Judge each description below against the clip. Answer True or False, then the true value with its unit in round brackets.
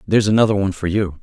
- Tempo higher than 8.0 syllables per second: True (8.3 syllables/s)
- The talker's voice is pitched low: True (100 Hz)